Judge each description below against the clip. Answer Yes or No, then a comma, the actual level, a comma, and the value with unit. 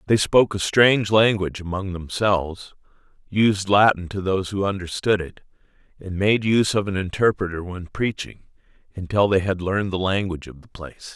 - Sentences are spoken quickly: No, average, 165 wpm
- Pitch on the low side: Yes, very low, 95 Hz